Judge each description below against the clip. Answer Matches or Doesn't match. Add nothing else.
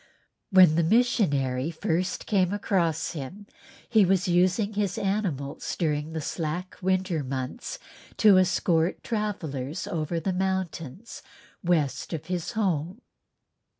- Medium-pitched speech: Matches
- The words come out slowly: Matches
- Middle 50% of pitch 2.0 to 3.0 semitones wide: Doesn't match